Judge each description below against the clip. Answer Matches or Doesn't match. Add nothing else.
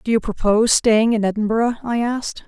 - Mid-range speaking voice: Doesn't match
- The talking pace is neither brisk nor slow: Matches